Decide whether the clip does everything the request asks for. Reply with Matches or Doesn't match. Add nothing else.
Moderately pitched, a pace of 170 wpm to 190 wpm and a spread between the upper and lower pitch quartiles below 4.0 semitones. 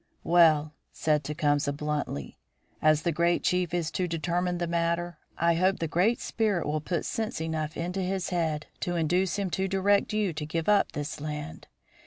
Matches